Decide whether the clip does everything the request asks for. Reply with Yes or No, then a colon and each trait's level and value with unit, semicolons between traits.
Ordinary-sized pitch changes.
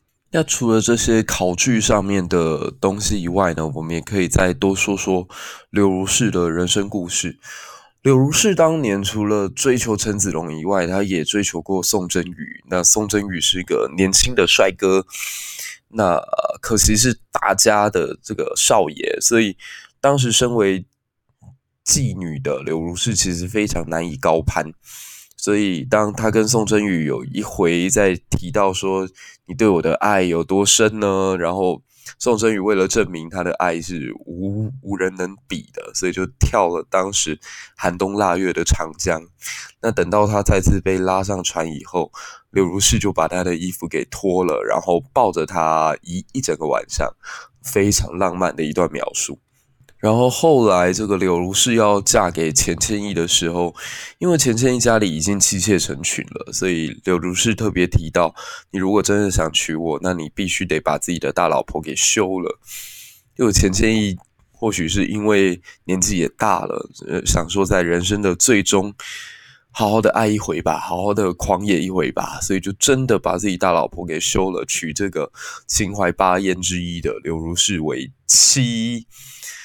Yes: average, 3.2 semitones